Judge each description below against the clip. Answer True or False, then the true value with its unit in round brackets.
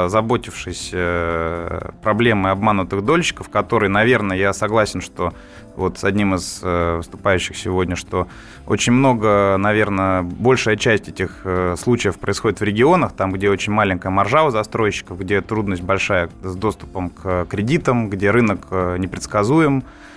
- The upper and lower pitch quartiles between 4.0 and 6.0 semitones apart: False (2.9 semitones)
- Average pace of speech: True (135 wpm)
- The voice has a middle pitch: False (95 Hz)